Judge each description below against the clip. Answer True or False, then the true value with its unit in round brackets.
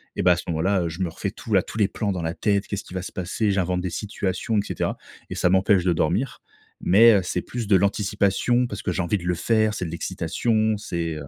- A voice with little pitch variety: False (3.1 semitones)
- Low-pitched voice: True (95 Hz)